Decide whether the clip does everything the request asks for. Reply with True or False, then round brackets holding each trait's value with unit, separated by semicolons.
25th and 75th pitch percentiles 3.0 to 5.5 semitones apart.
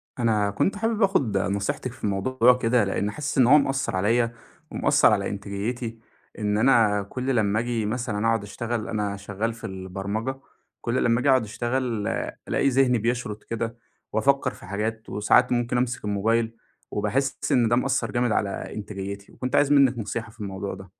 True (3.4 semitones)